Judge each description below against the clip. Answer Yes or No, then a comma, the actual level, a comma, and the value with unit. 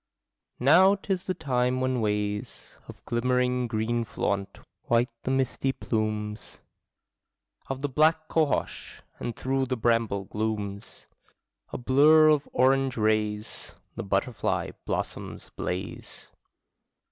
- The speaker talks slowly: Yes, slow, 110 wpm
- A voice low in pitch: Yes, low, 125 Hz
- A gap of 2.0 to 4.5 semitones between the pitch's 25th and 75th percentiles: Yes, average, 3.9 semitones